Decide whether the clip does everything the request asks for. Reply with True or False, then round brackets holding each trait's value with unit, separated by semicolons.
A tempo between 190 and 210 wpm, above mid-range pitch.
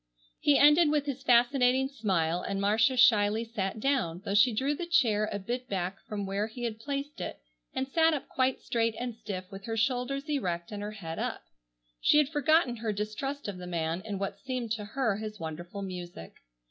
True (200 wpm; 225 Hz)